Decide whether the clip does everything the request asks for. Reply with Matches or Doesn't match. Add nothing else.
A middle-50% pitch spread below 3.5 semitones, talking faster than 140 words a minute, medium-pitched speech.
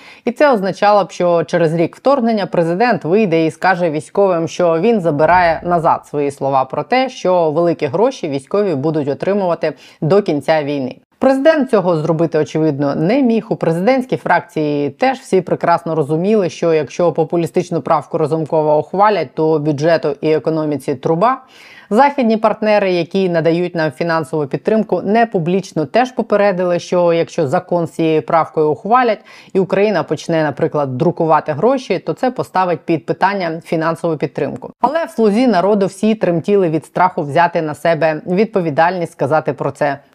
Doesn't match